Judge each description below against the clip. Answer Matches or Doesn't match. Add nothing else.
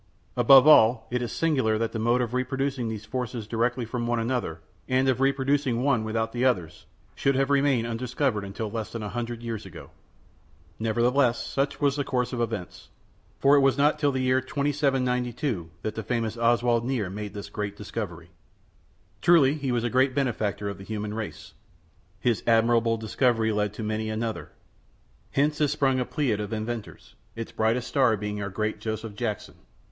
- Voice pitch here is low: Matches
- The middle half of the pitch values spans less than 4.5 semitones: Matches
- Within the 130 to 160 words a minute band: Doesn't match